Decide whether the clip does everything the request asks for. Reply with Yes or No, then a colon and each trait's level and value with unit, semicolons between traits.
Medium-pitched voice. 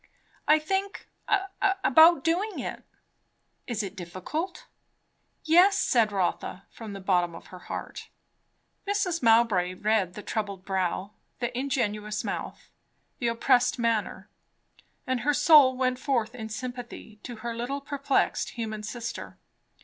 No: high, 235 Hz